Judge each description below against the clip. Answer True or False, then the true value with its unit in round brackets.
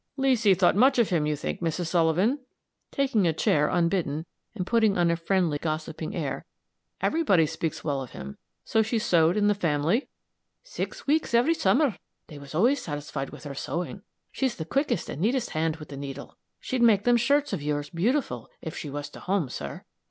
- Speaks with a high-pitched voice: False (175 Hz)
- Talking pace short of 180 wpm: False (190 wpm)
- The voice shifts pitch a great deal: True (7.5 semitones)